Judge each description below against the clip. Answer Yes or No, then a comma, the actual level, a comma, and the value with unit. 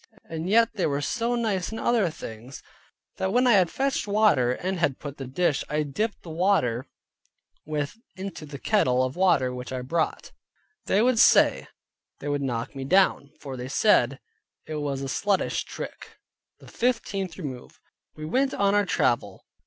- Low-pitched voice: No, medium, 160 Hz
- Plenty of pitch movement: Yes, wide, 7.0 semitones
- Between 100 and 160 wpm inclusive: No, average, 175 wpm